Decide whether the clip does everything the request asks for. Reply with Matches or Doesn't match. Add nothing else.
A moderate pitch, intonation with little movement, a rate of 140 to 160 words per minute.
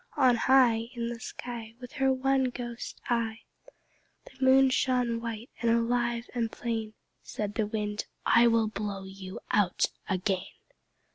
Doesn't match